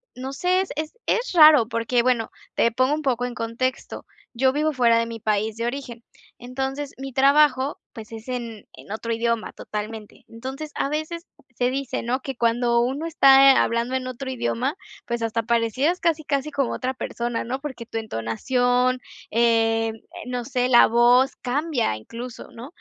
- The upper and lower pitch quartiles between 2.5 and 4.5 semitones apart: Yes, average, 2.8 semitones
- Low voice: No, very high, 250 Hz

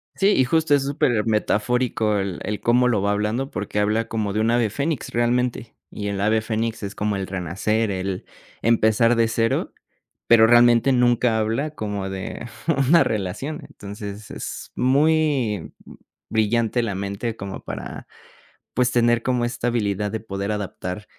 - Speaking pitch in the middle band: No, low, 110 Hz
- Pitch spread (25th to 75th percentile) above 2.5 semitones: Yes, average, 2.9 semitones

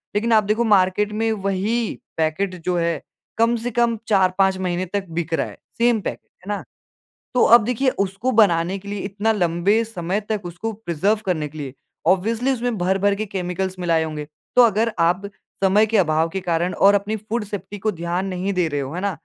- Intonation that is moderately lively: Yes, average, 3.7 semitones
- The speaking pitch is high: Yes, high, 195 Hz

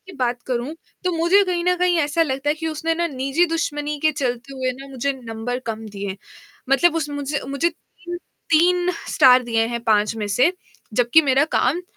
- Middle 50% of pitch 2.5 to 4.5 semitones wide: No, average, 5.0 semitones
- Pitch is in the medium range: No, very high, 280 Hz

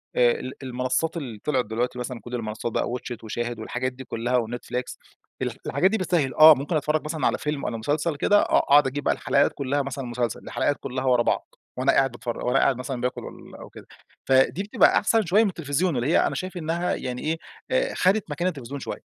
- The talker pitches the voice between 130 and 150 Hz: Yes, low, 135 Hz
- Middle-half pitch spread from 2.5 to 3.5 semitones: No, average, 4.1 semitones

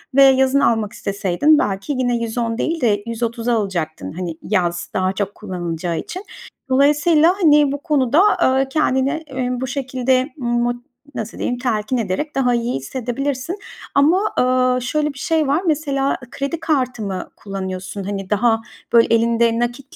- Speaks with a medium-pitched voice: No, high, 245 Hz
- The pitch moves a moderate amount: Yes, average, 4.8 semitones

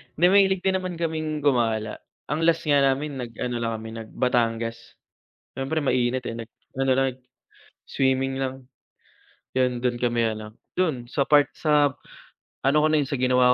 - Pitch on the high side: No, low, 135 Hz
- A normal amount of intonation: Yes, average, 3.7 semitones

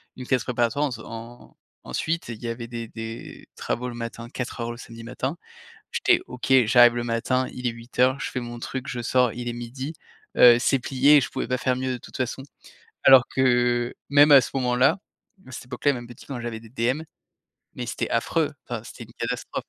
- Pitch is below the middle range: Yes, low, 125 Hz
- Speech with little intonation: Yes, narrow, 1.7 semitones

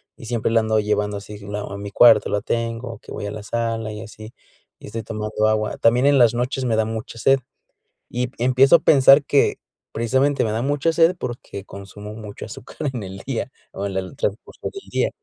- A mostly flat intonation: No, average, 3.0 semitones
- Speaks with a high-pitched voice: No, low, 115 Hz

